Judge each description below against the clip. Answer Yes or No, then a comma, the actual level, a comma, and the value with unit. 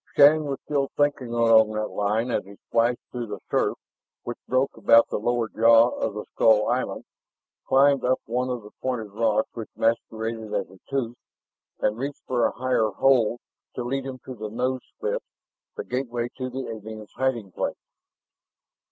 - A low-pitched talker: Yes, low, 120 Hz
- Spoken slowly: No, average, 175 wpm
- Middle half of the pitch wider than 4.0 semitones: No, average, 2.7 semitones